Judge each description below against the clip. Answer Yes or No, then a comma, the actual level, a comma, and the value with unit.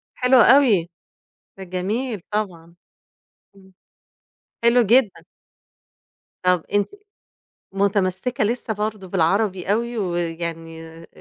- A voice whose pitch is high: Yes, high, 195 Hz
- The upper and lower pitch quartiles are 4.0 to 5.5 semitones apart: Yes, average, 4.3 semitones